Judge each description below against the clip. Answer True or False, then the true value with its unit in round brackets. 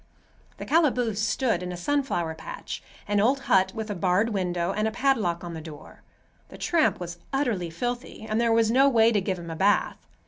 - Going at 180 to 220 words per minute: True (200 wpm)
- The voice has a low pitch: False (210 Hz)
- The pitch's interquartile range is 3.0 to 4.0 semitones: False (5.5 semitones)